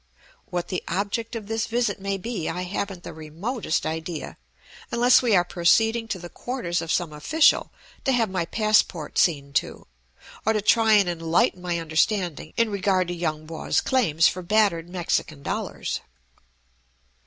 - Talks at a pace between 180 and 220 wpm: No, average, 160 wpm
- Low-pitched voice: No, medium, 185 Hz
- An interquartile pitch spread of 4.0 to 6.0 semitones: Yes, average, 4.8 semitones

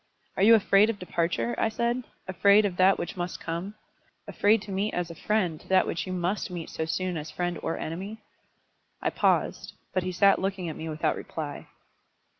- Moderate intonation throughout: Yes, average, 3.0 semitones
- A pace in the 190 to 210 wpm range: Yes, average, 195 wpm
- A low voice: No, medium, 185 Hz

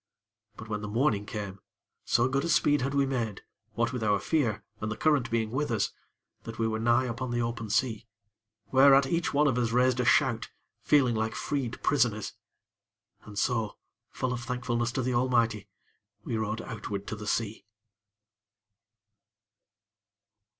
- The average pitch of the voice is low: Yes, low, 120 Hz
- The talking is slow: No, average, 165 wpm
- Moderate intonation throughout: Yes, average, 3.0 semitones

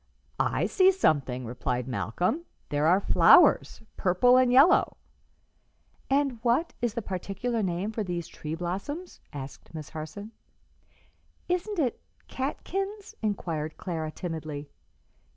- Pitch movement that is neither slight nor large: No, wide, 8.8 semitones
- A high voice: Yes, high, 195 Hz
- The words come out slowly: Yes, slow, 115 wpm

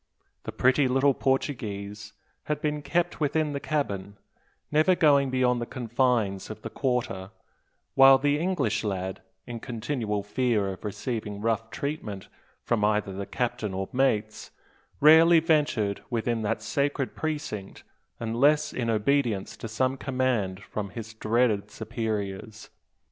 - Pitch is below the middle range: Yes, low, 120 Hz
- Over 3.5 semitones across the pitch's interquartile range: Yes, average, 4.9 semitones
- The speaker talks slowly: Yes, slow, 130 wpm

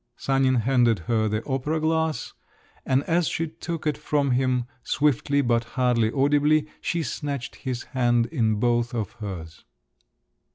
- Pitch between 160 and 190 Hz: No, low, 130 Hz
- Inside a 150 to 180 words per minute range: No, average, 140 wpm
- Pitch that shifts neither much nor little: Yes, average, 4.0 semitones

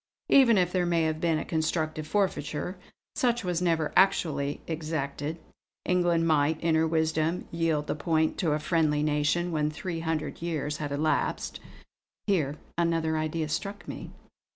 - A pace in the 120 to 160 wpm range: Yes, average, 155 wpm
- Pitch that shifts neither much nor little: No, narrow, 2.0 semitones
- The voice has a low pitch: No, medium, 160 Hz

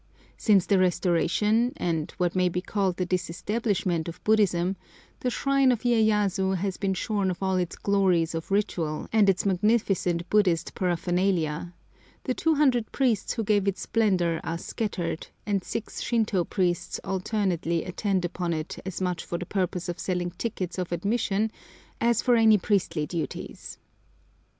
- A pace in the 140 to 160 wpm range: Yes, average, 150 wpm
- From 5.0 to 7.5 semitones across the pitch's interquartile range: No, average, 3.3 semitones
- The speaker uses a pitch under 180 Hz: No, high, 190 Hz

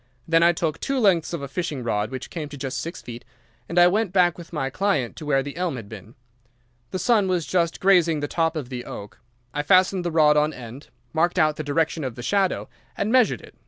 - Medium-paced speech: No, fast, 235 wpm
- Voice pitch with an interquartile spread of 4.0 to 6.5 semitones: Yes, average, 4.6 semitones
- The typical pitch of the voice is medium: Yes, medium, 160 Hz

